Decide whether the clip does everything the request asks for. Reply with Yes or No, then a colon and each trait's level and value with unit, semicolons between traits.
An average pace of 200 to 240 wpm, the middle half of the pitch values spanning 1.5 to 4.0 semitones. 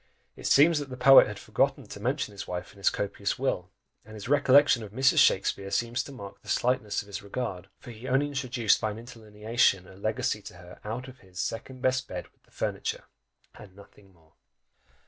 No: fast, 205 wpm; average, 4.4 semitones